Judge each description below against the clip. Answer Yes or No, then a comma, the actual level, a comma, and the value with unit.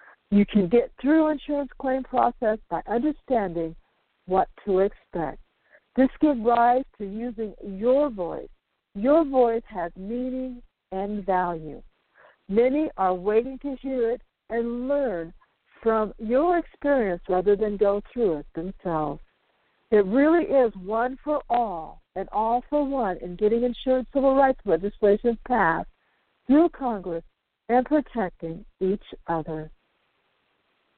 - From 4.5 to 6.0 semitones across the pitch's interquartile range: Yes, average, 5.2 semitones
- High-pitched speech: Yes, high, 230 Hz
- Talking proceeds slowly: Yes, slow, 125 wpm